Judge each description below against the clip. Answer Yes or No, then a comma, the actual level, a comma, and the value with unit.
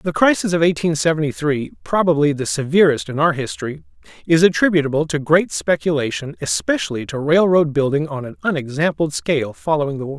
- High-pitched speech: No, medium, 150 Hz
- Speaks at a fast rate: No, average, 165 wpm